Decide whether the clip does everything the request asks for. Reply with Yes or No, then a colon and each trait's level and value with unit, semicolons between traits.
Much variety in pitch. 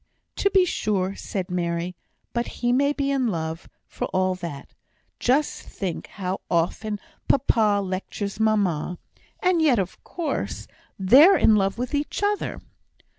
Yes: wide, 6.9 semitones